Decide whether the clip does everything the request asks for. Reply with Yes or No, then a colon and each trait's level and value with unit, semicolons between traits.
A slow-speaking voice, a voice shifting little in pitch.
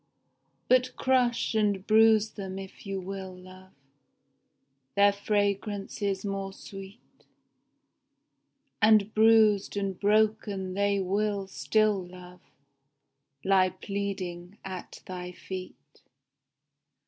Yes: slow, 95 wpm; narrow, 2.1 semitones